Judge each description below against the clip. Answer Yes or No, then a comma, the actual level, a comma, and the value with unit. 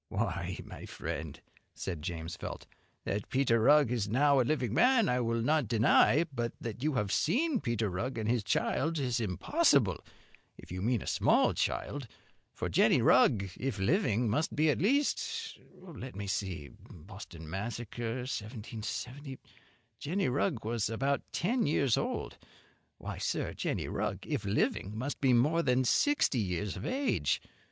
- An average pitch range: No, wide, 5.7 semitones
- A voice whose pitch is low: Yes, low, 120 Hz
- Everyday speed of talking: Yes, average, 155 wpm